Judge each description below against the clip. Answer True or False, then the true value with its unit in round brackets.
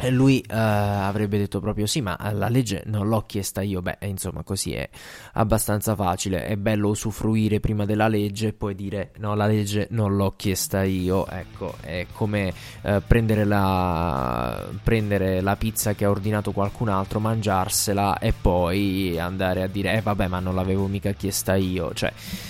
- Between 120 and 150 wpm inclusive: False (170 wpm)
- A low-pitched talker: True (100 Hz)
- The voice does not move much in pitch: True (2.0 semitones)